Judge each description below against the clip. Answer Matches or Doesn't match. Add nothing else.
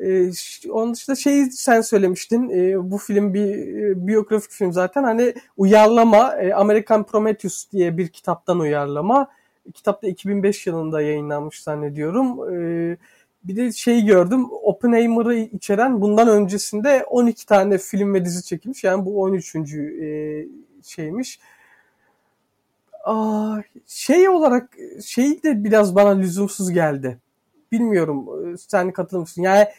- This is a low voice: Doesn't match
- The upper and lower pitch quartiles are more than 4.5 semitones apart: Doesn't match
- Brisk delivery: Doesn't match